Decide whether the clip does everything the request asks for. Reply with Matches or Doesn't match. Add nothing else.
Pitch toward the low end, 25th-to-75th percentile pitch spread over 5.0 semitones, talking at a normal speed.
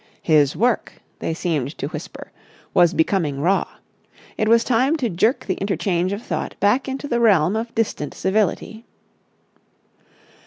Doesn't match